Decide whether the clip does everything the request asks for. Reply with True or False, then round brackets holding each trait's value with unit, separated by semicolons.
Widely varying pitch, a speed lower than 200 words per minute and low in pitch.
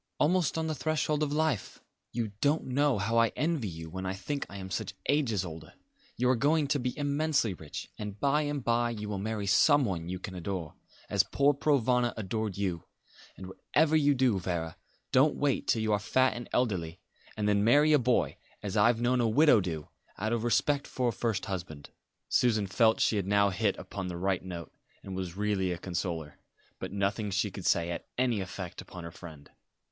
False (5.8 semitones; 205 wpm; 110 Hz)